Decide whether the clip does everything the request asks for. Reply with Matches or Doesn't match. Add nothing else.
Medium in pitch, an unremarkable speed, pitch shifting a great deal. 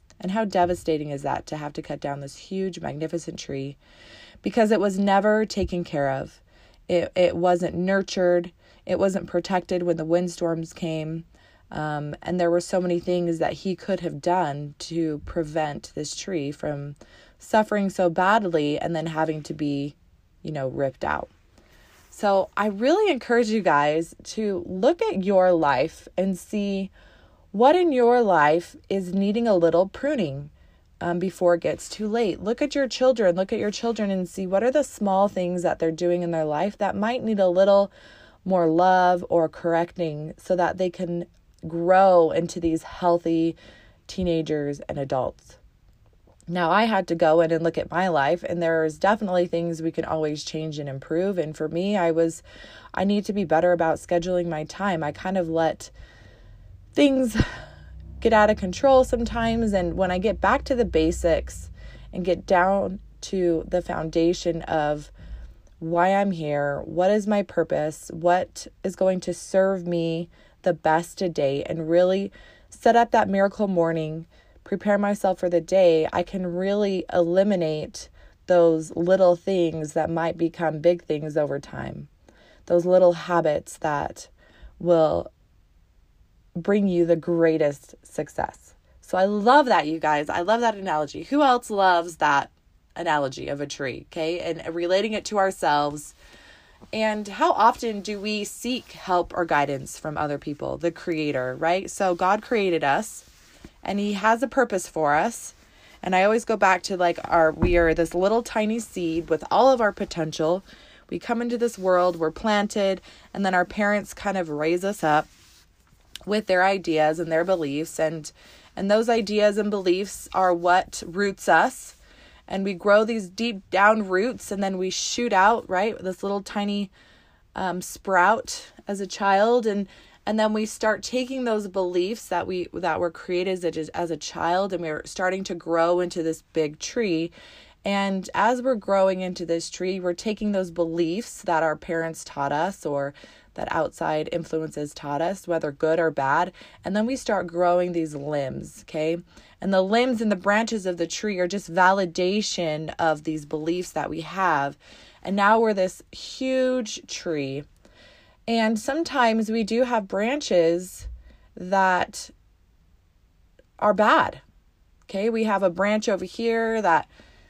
Doesn't match